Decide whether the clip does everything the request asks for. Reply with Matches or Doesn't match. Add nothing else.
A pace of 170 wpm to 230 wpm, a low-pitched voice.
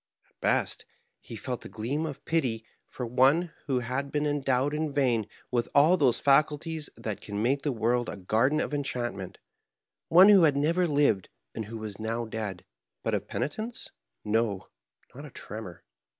Matches